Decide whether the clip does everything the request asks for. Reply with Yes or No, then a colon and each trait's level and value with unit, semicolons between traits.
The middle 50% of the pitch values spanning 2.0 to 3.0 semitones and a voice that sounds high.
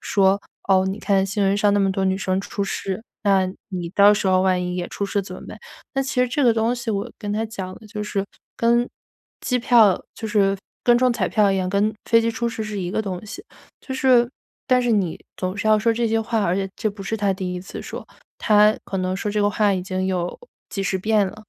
Yes: average, 2.7 semitones; high, 205 Hz